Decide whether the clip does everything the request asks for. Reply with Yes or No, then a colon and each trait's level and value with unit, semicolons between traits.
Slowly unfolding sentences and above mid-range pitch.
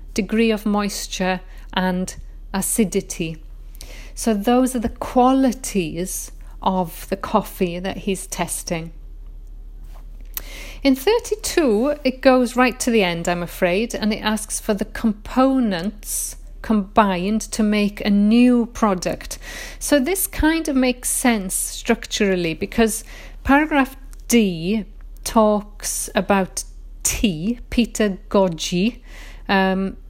Yes: slow, 110 wpm; high, 215 Hz